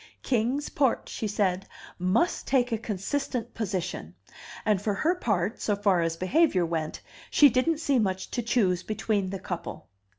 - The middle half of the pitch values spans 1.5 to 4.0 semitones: No, average, 5.2 semitones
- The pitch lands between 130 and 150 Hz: No, high, 210 Hz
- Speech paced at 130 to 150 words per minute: No, average, 160 wpm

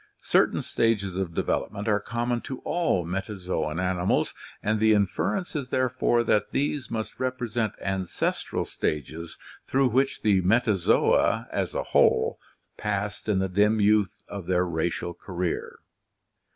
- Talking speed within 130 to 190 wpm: Yes, slow, 135 wpm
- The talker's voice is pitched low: Yes, low, 105 Hz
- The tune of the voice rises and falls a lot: No, average, 4.3 semitones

